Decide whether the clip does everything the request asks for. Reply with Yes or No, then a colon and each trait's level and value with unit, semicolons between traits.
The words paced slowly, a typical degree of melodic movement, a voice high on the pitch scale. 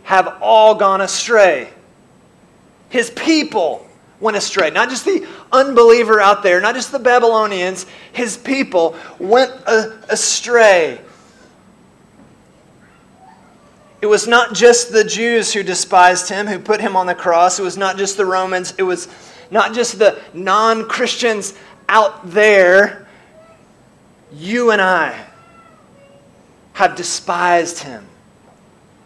Yes: slow, 120 wpm; average, 3.8 semitones; high, 210 Hz